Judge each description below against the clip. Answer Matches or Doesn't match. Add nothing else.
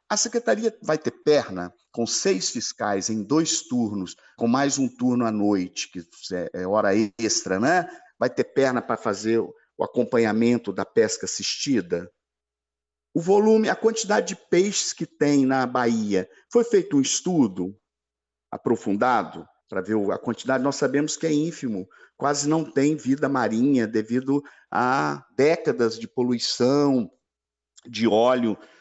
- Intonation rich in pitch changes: Matches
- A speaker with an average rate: Matches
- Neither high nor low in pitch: Doesn't match